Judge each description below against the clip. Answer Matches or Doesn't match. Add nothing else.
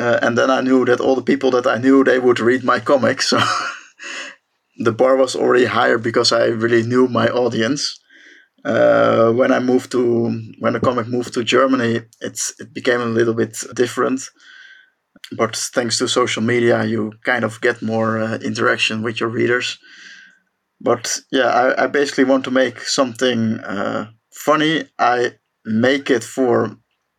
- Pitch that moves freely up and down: Doesn't match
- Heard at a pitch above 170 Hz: Doesn't match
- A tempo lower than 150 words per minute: Doesn't match